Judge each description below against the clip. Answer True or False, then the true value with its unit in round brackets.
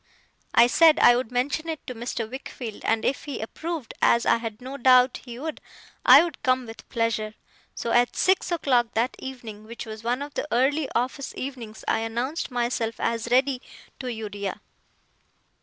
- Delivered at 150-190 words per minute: True (175 wpm)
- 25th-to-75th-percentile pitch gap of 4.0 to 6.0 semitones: False (2.9 semitones)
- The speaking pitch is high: True (245 Hz)